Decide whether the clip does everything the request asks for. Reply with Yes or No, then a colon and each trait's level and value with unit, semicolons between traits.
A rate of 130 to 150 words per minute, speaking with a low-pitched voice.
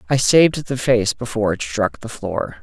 No: fast, 205 wpm; low, 115 Hz